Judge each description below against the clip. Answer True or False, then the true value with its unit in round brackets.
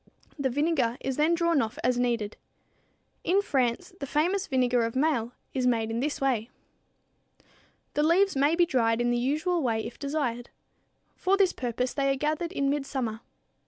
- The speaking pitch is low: False (270 Hz)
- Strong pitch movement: False (4.5 semitones)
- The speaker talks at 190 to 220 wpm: False (170 wpm)